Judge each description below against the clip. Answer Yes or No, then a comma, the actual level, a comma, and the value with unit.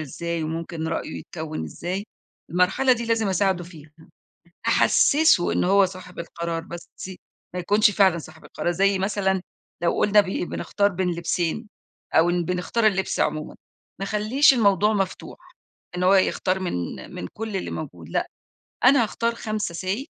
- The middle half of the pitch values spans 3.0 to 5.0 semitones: Yes, average, 3.4 semitones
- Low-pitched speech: No, high, 190 Hz